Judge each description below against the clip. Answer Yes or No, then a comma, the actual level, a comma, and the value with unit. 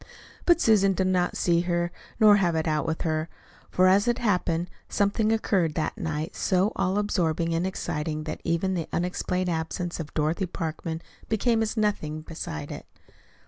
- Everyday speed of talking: Yes, average, 170 wpm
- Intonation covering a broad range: No, average, 3.7 semitones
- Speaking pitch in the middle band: Yes, medium, 175 Hz